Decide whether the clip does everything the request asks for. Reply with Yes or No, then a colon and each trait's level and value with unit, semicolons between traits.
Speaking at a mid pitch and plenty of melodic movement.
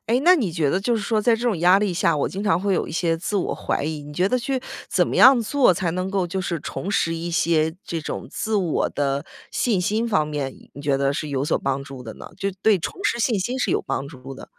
Yes: medium, 180 Hz; wide, 6.0 semitones